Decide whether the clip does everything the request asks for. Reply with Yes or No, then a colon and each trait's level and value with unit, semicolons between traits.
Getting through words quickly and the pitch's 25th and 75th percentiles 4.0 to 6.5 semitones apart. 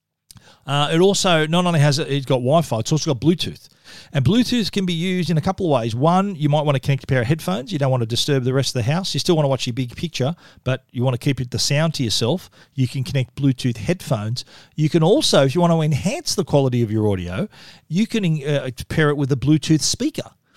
Yes: fast, 260 wpm; average, 4.5 semitones